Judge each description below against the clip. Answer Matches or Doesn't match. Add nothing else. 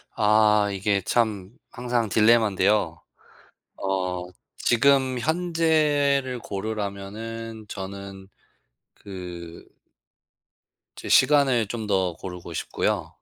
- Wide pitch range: Doesn't match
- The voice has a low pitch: Matches